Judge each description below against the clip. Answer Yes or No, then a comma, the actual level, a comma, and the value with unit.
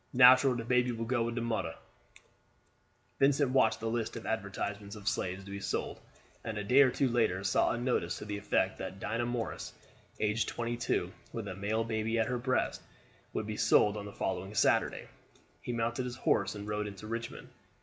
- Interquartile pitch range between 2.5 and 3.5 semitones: Yes, average, 2.8 semitones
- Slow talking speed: No, average, 200 wpm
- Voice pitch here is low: Yes, low, 115 Hz